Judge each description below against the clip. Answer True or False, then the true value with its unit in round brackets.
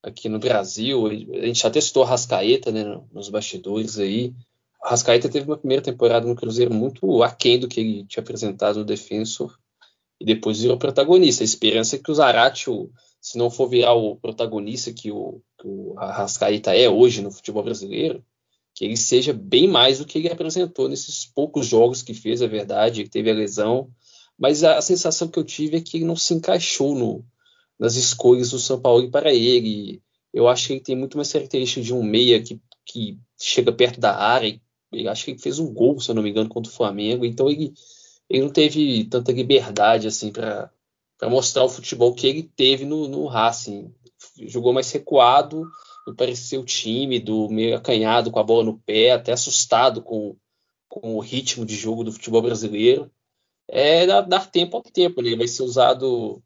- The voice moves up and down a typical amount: True (4.4 semitones)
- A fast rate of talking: True (190 wpm)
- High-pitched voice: False (125 Hz)